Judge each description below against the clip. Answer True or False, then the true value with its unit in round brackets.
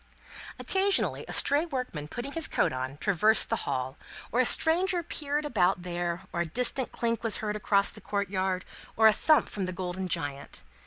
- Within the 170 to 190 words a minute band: True (180 wpm)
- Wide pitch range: True (7.1 semitones)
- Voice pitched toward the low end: False (210 Hz)